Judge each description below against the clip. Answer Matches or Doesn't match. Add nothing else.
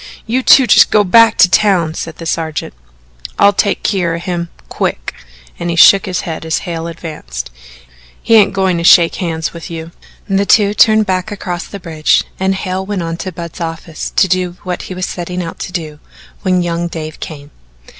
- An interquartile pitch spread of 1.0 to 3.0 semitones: Matches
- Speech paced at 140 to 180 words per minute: Doesn't match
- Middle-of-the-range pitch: Matches